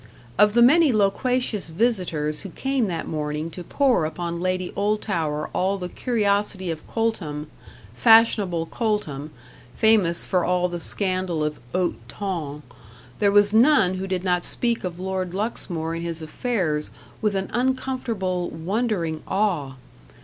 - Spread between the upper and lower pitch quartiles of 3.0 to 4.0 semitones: No, average, 4.5 semitones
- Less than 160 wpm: Yes, average, 140 wpm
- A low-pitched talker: No, medium, 185 Hz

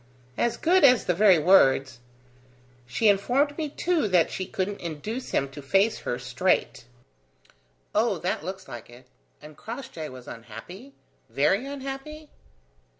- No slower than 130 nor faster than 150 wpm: Yes, average, 140 wpm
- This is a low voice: No, high, 195 Hz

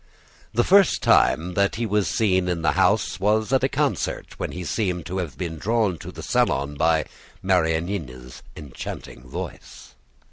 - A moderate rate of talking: Yes, average, 165 wpm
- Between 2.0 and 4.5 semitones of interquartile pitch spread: No, average, 5.0 semitones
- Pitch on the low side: Yes, very low, 90 Hz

